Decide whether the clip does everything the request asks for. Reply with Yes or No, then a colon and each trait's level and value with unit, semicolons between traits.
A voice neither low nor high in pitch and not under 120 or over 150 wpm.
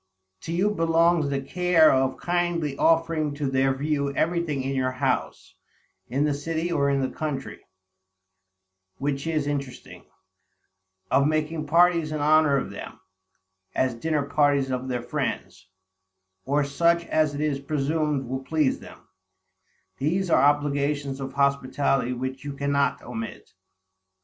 Yes: medium, 145 Hz; average, 140 wpm